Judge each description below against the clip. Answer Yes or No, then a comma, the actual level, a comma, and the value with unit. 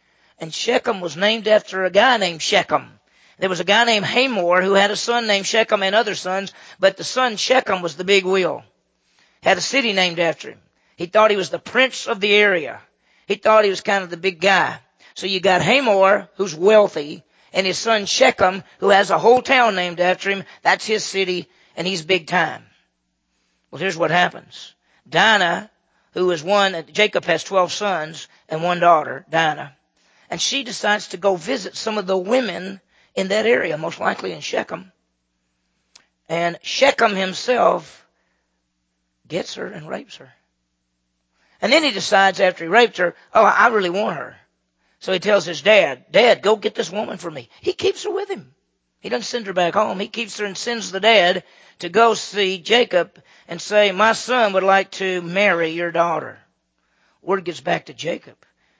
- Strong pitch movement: No, average, 3.8 semitones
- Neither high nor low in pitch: No, high, 195 Hz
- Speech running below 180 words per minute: No, average, 190 wpm